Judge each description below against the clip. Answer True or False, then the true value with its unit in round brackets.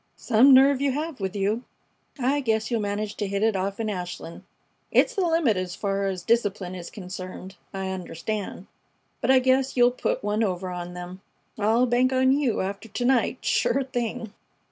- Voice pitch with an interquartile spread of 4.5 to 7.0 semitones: True (4.9 semitones)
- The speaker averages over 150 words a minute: True (185 wpm)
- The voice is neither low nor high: False (215 Hz)